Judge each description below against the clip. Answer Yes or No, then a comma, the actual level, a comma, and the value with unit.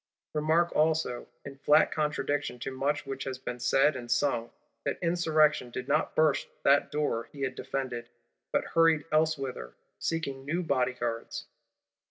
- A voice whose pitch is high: No, medium, 140 Hz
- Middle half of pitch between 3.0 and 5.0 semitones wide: Yes, average, 3.3 semitones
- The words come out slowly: No, average, 145 wpm